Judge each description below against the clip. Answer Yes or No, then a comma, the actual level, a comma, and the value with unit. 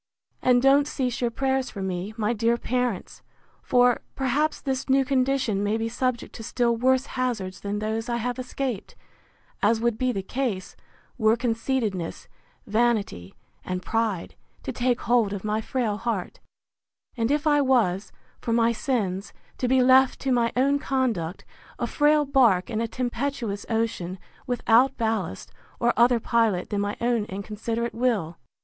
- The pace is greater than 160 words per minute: No, average, 155 wpm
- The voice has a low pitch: No, high, 235 Hz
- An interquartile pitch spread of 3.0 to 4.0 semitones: Yes, average, 3.3 semitones